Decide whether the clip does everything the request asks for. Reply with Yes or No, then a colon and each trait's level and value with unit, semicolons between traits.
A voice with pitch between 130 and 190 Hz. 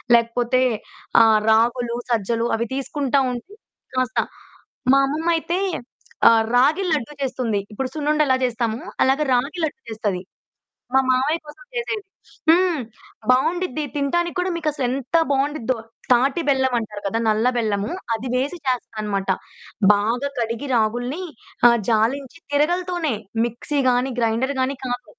No: very high, 255 Hz